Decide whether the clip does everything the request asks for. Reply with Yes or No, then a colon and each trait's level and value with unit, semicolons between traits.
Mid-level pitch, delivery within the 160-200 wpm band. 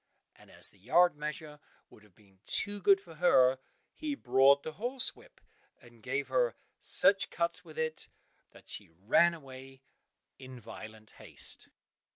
No: medium, 150 Hz; average, 150 wpm